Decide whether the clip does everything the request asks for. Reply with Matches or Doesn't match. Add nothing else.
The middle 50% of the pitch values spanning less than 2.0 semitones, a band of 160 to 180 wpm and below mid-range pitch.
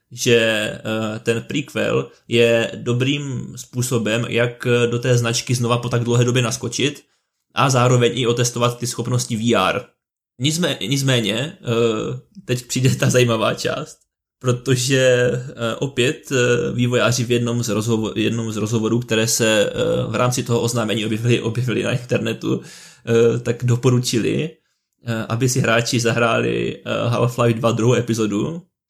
Doesn't match